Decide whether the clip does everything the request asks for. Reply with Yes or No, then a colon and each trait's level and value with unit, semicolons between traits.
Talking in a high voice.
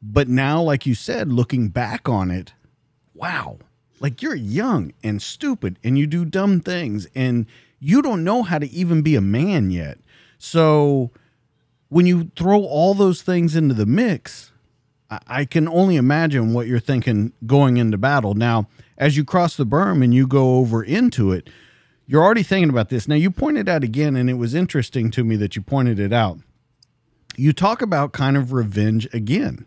No: low, 135 Hz